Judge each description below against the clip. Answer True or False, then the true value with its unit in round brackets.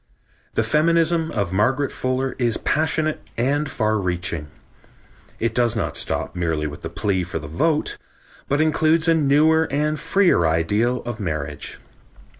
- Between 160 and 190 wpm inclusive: False (145 wpm)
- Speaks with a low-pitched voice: True (125 Hz)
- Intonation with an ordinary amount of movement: False (8.6 semitones)